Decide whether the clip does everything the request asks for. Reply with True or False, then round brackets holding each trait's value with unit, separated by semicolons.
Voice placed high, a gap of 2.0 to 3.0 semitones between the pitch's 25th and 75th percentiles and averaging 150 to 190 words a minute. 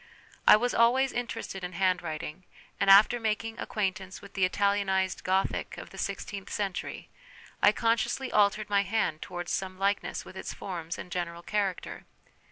True (195 Hz; 2.5 semitones; 160 wpm)